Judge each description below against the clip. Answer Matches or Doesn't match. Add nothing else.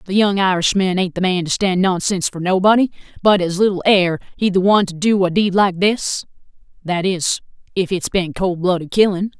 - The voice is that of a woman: Matches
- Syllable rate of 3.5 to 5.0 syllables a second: Doesn't match